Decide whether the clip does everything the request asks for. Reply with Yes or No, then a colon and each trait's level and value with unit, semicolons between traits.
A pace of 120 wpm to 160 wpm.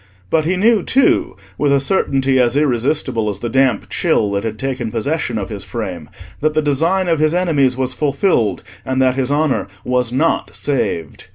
No: average, 185 wpm